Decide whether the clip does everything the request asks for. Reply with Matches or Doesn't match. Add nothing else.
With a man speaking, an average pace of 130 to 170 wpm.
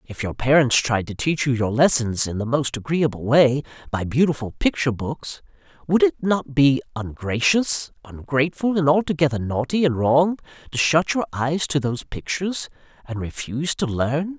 Matches